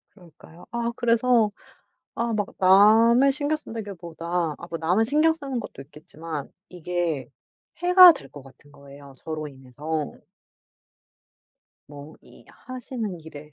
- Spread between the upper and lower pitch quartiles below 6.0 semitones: No, wide, 7.5 semitones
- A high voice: No, medium, 180 Hz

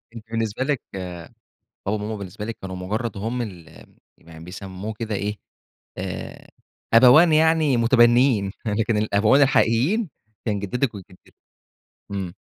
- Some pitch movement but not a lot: Yes, average, 4.0 semitones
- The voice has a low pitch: Yes, low, 110 Hz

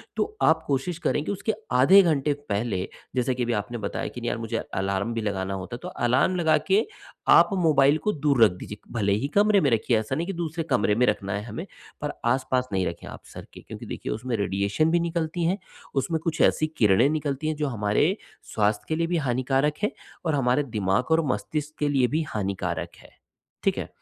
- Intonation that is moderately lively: No, wide, 6.7 semitones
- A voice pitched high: No, low, 135 Hz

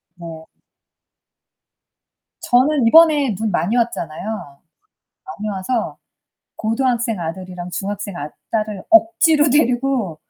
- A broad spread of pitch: Yes, wide, 6.3 semitones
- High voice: Yes, high, 220 Hz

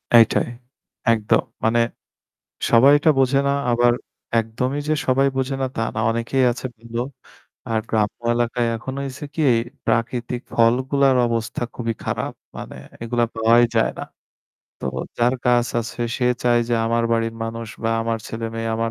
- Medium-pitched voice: No, low, 120 Hz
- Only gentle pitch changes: Yes, narrow, 1.9 semitones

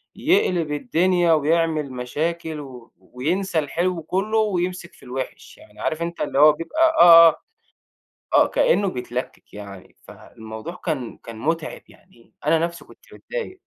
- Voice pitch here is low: No, medium, 165 Hz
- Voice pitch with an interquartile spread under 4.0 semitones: No, average, 4.7 semitones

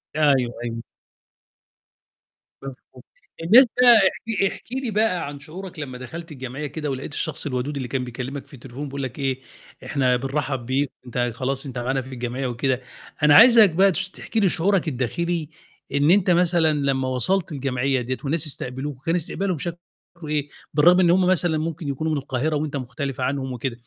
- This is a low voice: No, medium, 145 Hz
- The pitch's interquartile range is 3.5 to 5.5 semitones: Yes, average, 4.6 semitones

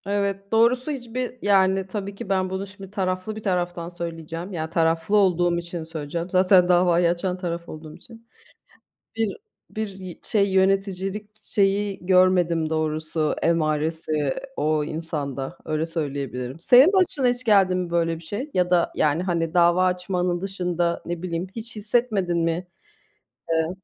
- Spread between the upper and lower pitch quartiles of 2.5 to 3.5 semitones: Yes, average, 3.1 semitones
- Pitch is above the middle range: No, medium, 180 Hz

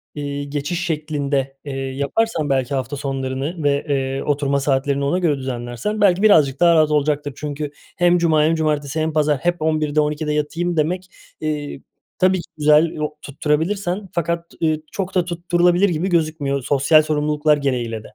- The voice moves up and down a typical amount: Yes, average, 3.2 semitones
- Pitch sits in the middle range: Yes, medium, 150 Hz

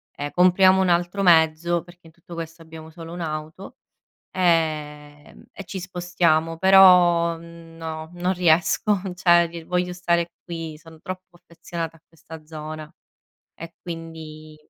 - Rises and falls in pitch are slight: Yes, narrow, 1.7 semitones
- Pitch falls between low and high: Yes, medium, 170 Hz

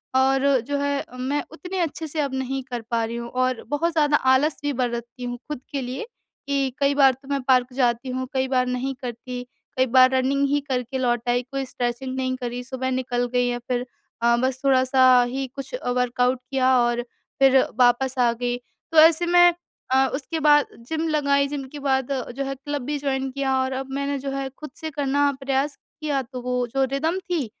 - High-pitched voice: Yes, very high, 265 Hz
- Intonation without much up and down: Yes, narrow, 2.0 semitones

